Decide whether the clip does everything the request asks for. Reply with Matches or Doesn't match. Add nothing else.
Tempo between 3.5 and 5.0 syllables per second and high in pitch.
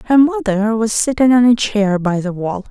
Matches